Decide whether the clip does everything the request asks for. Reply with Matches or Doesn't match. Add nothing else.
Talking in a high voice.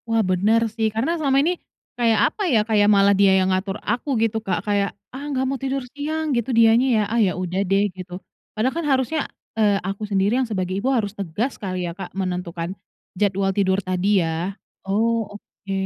Matches